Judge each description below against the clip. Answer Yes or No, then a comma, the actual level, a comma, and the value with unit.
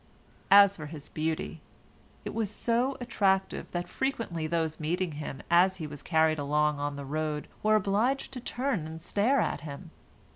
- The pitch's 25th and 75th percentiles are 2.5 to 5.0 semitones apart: No, wide, 5.5 semitones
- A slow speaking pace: No, average, 170 wpm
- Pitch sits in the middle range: Yes, medium, 170 Hz